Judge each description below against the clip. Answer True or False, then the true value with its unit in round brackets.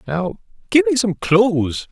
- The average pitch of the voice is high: False (170 Hz)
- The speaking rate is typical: True (155 wpm)